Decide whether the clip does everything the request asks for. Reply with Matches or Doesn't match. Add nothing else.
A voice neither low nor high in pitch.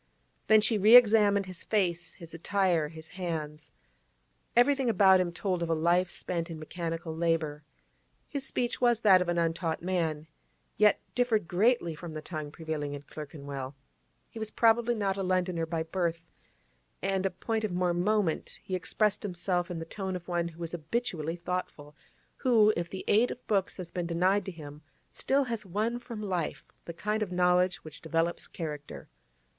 Matches